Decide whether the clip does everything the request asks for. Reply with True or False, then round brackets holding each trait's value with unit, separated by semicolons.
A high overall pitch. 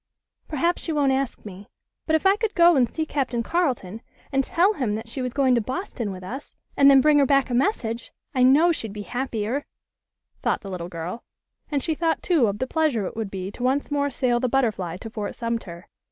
True (255 Hz)